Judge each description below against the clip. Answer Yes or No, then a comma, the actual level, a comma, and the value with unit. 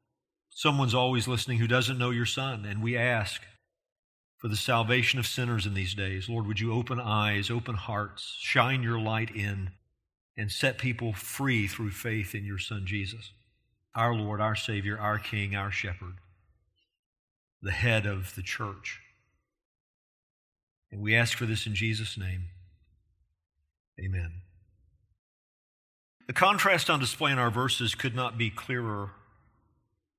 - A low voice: Yes, low, 110 Hz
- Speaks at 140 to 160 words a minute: Yes, average, 145 wpm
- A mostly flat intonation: No, average, 3.2 semitones